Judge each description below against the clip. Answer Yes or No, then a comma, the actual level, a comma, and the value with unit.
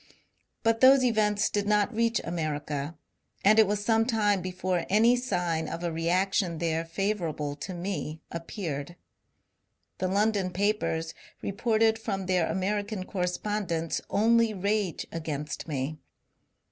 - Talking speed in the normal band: No, slow, 130 wpm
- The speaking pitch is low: No, high, 190 Hz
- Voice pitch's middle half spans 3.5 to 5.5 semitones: Yes, average, 4.3 semitones